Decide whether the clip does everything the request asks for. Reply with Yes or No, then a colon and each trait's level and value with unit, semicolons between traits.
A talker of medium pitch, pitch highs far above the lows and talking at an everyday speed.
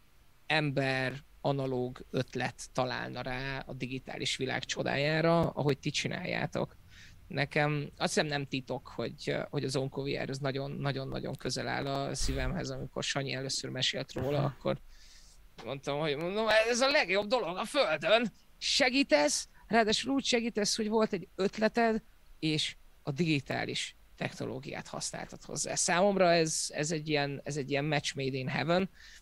Yes: medium, 150 Hz; wide, 6.3 semitones; average, 140 wpm